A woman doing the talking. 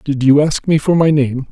No: male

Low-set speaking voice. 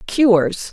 No: high, 210 Hz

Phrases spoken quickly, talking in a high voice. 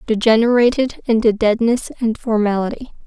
No: slow, 100 wpm; high, 225 Hz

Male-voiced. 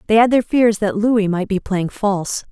No: female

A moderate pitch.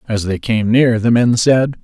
No: low, 115 Hz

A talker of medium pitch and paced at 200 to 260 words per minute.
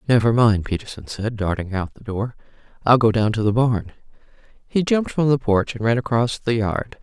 No: low, 115 Hz; fast, 205 wpm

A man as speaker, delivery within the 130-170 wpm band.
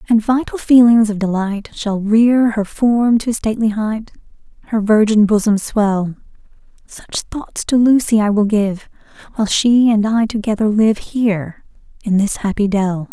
No: female; average, 155 wpm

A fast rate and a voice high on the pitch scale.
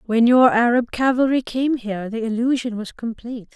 No: average, 170 wpm; high, 235 Hz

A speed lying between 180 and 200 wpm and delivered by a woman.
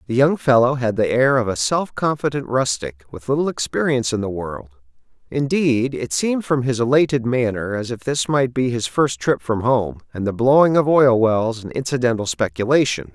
No: average, 195 wpm; male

